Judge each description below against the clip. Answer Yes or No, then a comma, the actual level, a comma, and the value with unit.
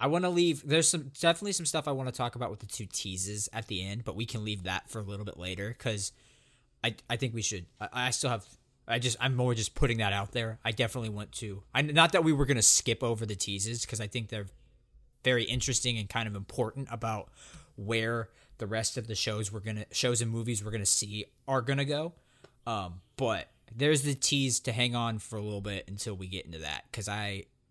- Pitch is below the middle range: Yes, low, 115 Hz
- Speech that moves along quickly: Yes, fast, 240 wpm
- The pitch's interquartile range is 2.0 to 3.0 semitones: No, average, 3.6 semitones